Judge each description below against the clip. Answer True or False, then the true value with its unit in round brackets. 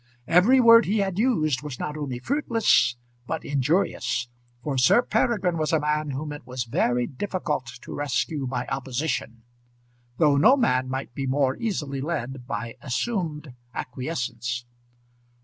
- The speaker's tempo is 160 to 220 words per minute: False (145 wpm)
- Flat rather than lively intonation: False (5.1 semitones)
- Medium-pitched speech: True (145 Hz)